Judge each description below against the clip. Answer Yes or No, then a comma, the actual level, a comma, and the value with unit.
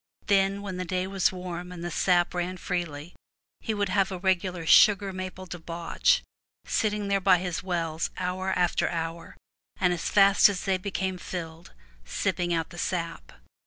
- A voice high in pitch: No, medium, 180 Hz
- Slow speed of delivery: No, average, 165 wpm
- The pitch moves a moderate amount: No, narrow, 1.9 semitones